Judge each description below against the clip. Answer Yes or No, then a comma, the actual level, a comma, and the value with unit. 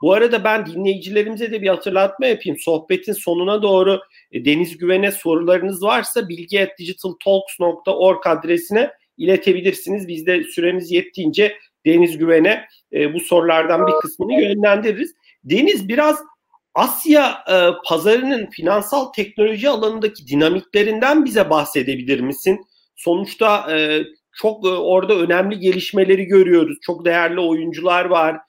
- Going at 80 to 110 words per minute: Yes, average, 105 wpm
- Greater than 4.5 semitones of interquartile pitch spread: No, average, 3.5 semitones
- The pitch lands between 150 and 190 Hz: Yes, medium, 185 Hz